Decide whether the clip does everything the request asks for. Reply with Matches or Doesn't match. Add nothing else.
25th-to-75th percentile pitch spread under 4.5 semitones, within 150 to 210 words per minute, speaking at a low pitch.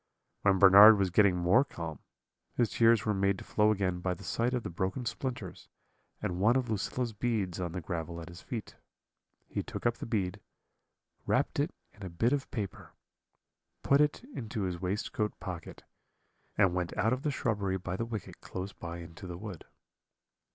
Matches